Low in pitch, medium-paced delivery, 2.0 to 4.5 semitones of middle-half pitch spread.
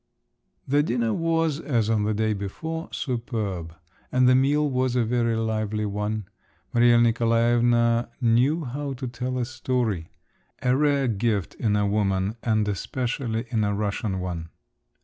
Yes: low, 115 Hz; average, 150 wpm; average, 3.2 semitones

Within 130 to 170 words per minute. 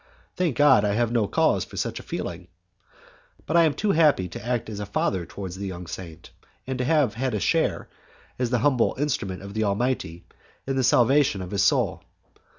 No: fast, 205 wpm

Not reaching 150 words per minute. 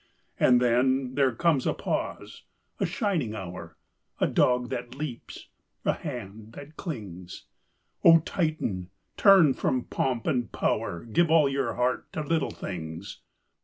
Yes: slow, 135 wpm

